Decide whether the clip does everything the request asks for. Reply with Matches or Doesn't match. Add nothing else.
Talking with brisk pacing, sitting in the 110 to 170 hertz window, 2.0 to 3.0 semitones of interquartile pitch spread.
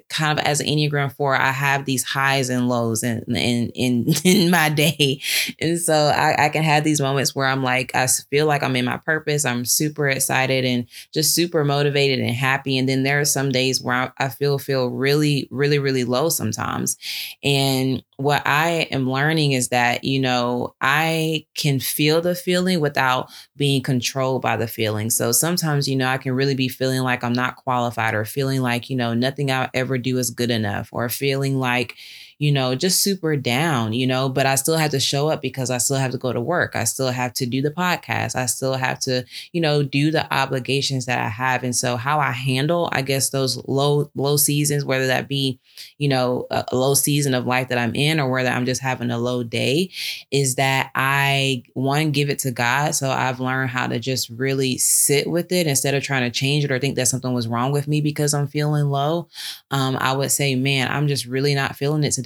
Matches